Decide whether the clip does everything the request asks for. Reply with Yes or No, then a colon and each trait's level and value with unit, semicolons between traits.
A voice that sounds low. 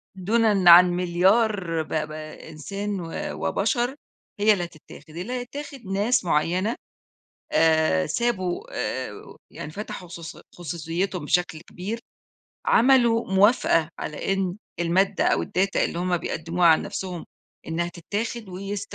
No: medium, 180 Hz